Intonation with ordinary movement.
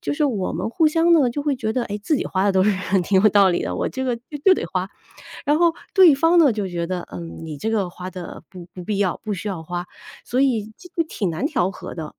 No: wide, 7.3 semitones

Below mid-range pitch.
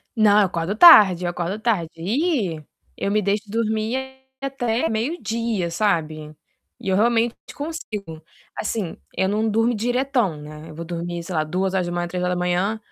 No: high, 205 Hz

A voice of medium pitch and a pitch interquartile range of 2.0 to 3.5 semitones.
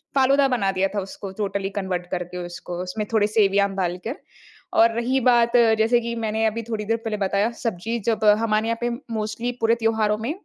No: high, 220 Hz; average, 2.8 semitones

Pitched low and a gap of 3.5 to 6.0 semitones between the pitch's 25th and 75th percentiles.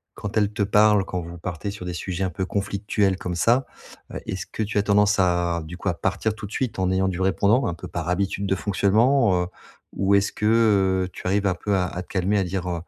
No: very low, 95 Hz; narrow, 2.4 semitones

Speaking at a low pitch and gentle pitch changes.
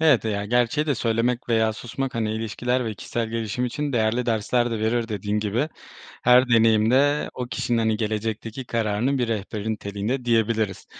Yes: low, 115 Hz; narrow, 2.2 semitones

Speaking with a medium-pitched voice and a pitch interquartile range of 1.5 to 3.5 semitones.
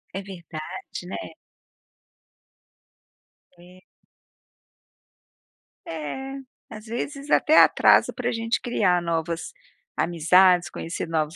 No: medium, 180 Hz; average, 4.8 semitones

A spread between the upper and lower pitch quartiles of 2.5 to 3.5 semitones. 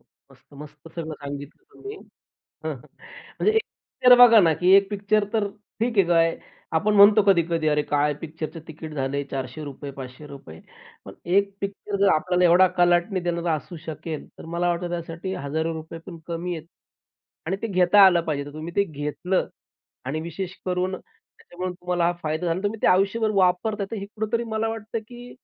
No: average, 4.1 semitones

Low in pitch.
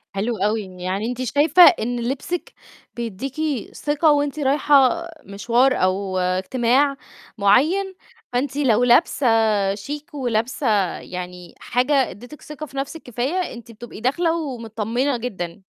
No: very high, 250 Hz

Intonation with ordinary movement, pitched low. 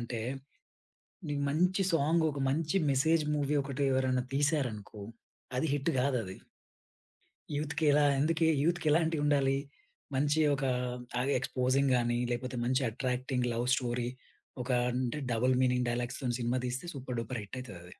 Yes: average, 3.0 semitones; low, 130 Hz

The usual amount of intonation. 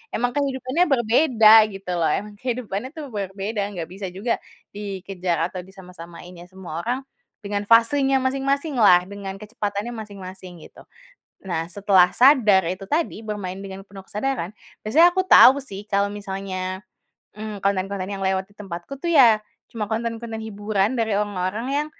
Yes: average, 3.5 semitones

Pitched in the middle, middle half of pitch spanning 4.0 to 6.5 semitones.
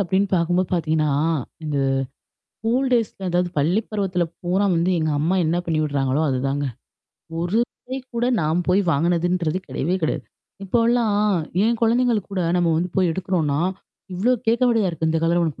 Yes: medium, 175 Hz; average, 4.4 semitones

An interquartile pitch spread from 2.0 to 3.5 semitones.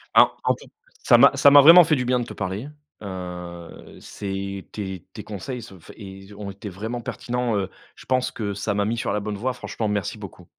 No: average, 4.0 semitones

